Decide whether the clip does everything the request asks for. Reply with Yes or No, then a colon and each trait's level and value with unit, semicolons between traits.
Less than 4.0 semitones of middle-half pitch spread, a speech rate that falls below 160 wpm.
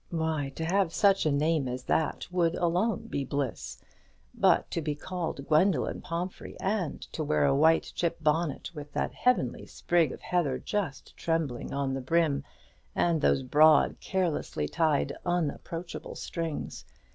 Yes: average, 3.4 semitones; average, 150 wpm